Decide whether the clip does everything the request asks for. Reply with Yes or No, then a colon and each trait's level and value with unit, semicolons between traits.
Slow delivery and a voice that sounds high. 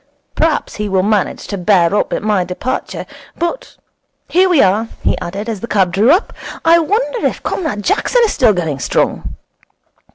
No: average, 175 wpm; high, 210 Hz